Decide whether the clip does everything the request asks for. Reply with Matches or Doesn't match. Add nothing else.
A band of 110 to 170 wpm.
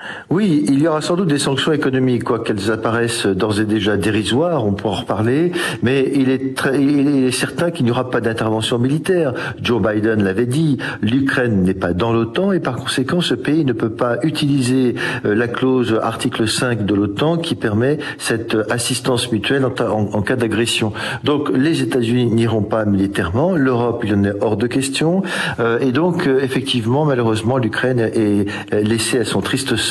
Doesn't match